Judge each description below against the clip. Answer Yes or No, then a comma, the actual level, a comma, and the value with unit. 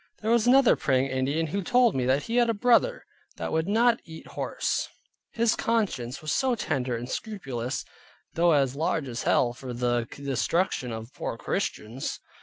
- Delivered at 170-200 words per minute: Yes, average, 175 wpm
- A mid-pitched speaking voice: Yes, medium, 155 Hz